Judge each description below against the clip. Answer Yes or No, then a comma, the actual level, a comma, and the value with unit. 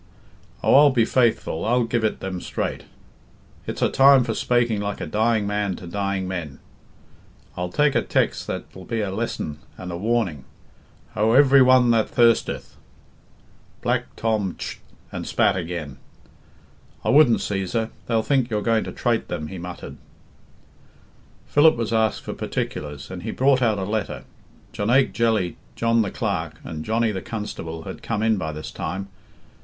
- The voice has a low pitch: Yes, low, 110 Hz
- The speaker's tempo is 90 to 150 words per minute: No, average, 165 wpm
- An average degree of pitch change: Yes, average, 4.2 semitones